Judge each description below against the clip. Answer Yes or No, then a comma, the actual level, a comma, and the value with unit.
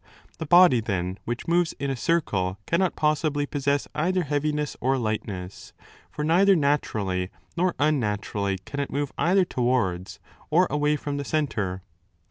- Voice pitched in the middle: Yes, medium, 145 Hz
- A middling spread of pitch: No, wide, 6.5 semitones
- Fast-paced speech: No, average, 145 wpm